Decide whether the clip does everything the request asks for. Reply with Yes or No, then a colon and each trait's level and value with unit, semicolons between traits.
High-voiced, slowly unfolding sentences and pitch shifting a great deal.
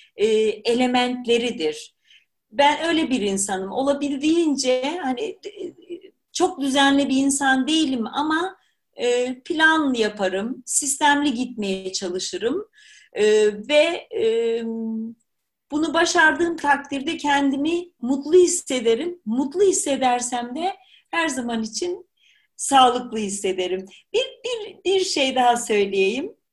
Yes: very high, 285 Hz; slow, 90 wpm; wide, 6.2 semitones